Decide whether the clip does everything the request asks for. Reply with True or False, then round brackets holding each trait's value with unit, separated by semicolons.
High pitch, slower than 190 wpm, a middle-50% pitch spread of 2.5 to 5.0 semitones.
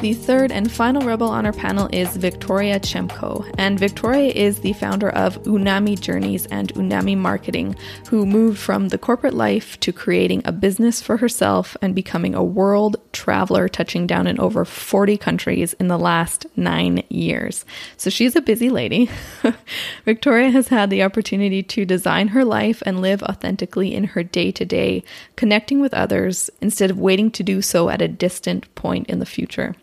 True (200 Hz; 175 wpm; 3.6 semitones)